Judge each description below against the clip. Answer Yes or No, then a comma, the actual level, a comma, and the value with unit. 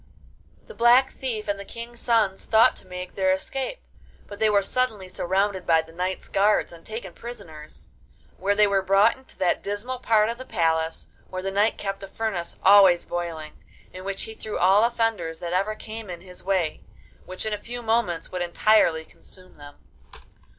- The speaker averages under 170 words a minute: No, average, 185 wpm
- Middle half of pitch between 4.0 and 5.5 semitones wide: No, average, 3.4 semitones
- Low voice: No, high, 195 Hz